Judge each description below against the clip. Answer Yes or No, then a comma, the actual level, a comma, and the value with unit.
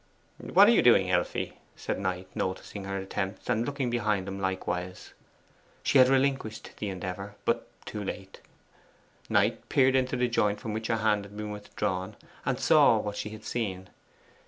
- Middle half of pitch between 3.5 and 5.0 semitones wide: No, average, 3.0 semitones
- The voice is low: Yes, low, 105 Hz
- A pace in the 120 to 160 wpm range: No, average, 170 wpm